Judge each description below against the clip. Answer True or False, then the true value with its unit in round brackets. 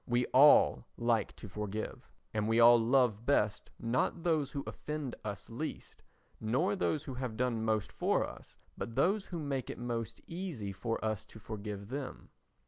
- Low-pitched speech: True (120 Hz)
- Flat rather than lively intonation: False (4.4 semitones)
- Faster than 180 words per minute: False (170 wpm)